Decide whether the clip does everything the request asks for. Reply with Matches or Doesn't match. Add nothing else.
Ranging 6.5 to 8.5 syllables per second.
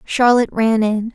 Doesn't match